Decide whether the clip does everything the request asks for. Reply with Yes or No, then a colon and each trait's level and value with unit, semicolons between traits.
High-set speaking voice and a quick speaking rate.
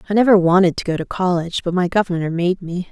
No: medium, 180 Hz; fast, 245 wpm